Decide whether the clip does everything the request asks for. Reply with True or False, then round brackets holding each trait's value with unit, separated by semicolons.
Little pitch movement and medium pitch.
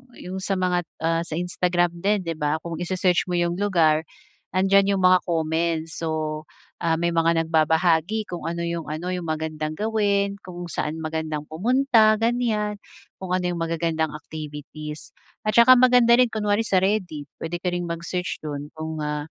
False (3.4 semitones; 170 Hz)